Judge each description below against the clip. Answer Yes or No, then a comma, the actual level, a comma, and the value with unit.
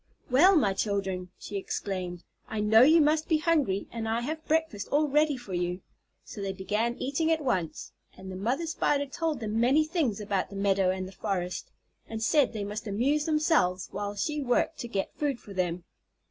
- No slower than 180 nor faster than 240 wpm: Yes, average, 195 wpm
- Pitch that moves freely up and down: Yes, wide, 7.4 semitones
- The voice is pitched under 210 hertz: No, high, 225 Hz